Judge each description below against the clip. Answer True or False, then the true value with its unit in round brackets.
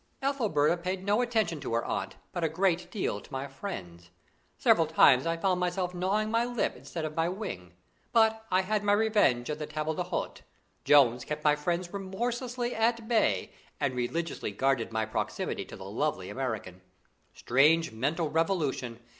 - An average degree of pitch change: False (7.2 semitones)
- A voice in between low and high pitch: True (165 Hz)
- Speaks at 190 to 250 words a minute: False (170 wpm)